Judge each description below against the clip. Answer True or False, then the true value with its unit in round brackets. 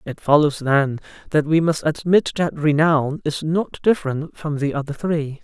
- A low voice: False (150 Hz)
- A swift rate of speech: False (175 wpm)